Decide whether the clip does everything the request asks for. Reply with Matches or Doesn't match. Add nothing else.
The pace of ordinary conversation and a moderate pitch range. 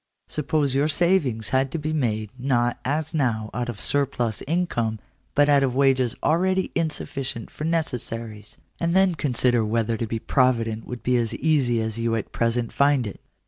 Matches